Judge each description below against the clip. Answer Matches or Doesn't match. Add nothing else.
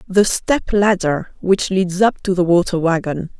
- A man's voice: Doesn't match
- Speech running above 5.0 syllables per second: Doesn't match